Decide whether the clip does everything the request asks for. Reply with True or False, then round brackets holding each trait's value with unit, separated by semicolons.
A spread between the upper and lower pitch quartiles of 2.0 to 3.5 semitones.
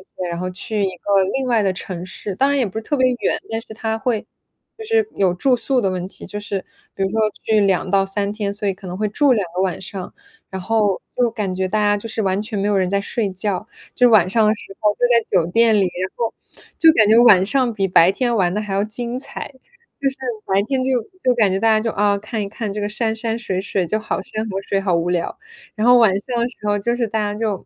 True (3.0 semitones)